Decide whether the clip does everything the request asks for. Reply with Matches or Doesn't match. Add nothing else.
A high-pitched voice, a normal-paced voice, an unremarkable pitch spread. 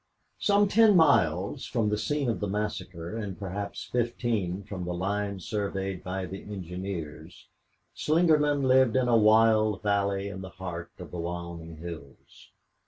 Doesn't match